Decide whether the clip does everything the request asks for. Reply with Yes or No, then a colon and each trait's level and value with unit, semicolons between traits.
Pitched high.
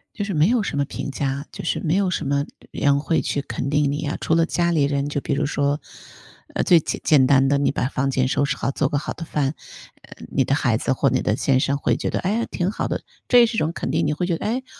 No: medium, 145 Hz